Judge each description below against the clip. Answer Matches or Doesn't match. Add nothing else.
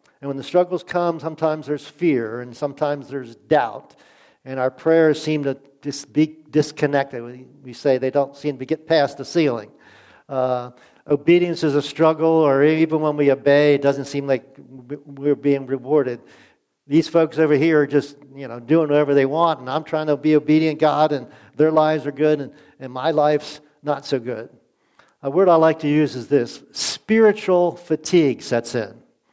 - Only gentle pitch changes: Matches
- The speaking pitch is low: Doesn't match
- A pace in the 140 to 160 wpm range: Doesn't match